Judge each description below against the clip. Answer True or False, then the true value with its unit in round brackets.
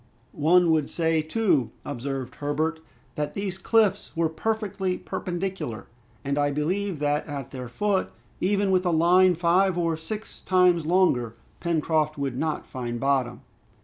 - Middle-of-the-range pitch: True (165 Hz)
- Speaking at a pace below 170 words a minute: True (145 wpm)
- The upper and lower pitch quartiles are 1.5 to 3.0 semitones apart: False (4.5 semitones)